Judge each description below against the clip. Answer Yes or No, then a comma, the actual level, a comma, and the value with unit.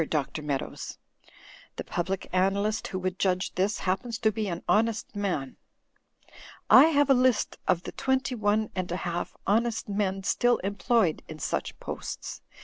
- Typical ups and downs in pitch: Yes, average, 3.6 semitones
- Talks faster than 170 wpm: No, average, 155 wpm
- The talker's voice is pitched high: Yes, high, 200 Hz